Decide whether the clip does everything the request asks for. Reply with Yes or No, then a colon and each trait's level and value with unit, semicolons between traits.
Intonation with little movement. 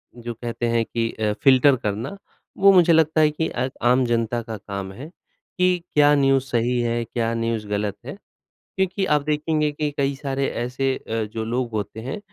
No: average, 4.4 semitones